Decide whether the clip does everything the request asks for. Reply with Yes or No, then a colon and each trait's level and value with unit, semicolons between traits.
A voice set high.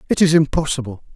No: medium, 140 Hz